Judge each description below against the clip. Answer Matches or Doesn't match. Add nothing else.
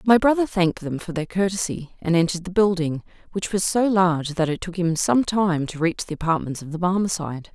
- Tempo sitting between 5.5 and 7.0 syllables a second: Matches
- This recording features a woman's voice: Matches